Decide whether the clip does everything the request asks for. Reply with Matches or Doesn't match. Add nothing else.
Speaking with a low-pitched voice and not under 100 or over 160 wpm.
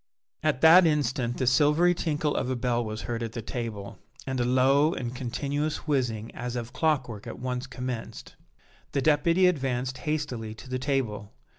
Doesn't match